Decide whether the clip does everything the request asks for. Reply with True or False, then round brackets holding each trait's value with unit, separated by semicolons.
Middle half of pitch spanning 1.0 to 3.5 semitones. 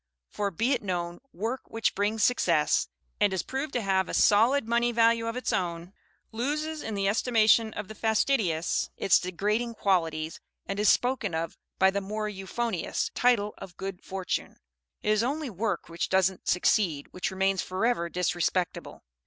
False (4.0 semitones)